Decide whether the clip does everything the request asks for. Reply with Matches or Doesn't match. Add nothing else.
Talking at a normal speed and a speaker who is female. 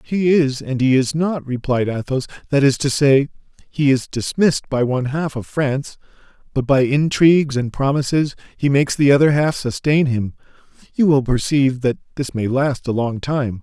Doesn't match